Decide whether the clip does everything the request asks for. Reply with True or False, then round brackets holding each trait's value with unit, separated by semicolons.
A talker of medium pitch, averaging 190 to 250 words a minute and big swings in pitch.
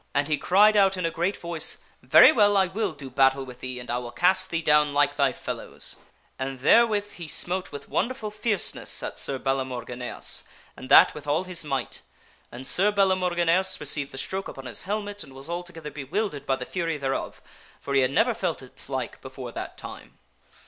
True (155 Hz; 205 wpm; 5.9 semitones)